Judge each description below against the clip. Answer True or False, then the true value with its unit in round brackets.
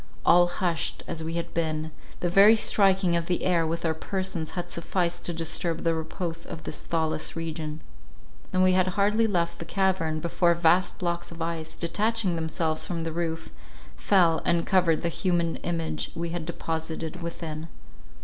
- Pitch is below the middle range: False (170 Hz)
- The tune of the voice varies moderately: False (1.8 semitones)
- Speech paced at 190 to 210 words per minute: False (170 wpm)